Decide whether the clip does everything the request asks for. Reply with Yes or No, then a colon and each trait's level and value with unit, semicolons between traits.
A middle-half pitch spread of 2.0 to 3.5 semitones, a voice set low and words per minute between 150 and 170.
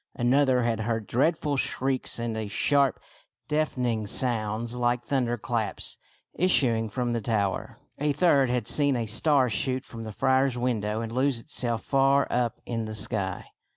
Yes: average, 3.2 semitones; low, 120 Hz; average, 155 wpm